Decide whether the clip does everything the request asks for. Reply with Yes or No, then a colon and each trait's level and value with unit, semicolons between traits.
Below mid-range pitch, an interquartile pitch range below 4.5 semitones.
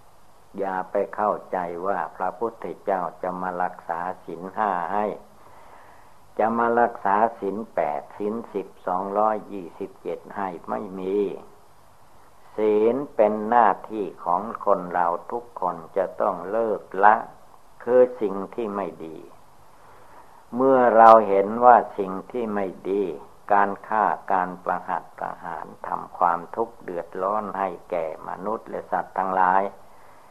Yes: low, 100 Hz; average, 3.5 semitones